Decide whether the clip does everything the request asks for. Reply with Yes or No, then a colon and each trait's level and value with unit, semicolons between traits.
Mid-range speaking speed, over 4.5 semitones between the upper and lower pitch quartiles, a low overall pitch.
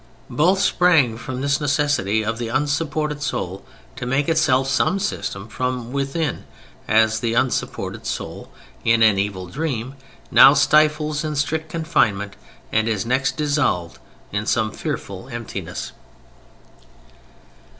No: slow, 125 wpm; average, 5.2 semitones; low, 130 Hz